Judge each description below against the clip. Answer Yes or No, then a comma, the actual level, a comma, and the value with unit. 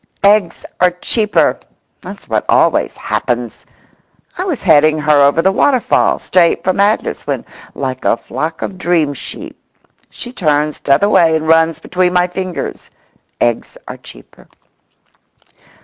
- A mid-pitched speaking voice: Yes, medium, 170 Hz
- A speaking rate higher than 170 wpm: No, slow, 135 wpm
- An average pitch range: Yes, average, 4.0 semitones